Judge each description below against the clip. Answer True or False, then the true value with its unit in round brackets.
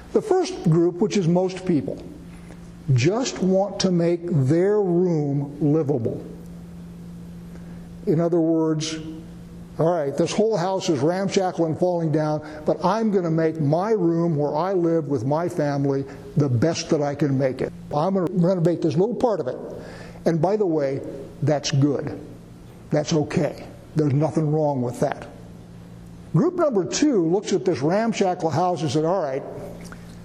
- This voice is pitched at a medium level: True (165 Hz)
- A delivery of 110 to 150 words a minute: False (160 wpm)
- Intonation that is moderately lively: True (3.3 semitones)